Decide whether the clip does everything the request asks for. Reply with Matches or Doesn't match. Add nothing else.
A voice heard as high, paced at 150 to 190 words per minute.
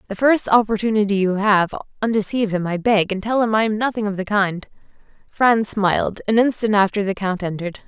Doesn't match